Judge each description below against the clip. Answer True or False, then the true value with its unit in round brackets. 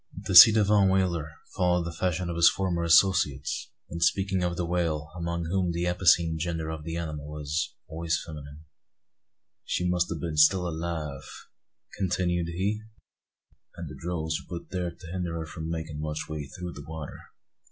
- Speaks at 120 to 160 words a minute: False (175 wpm)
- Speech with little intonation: True (2.0 semitones)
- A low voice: True (85 Hz)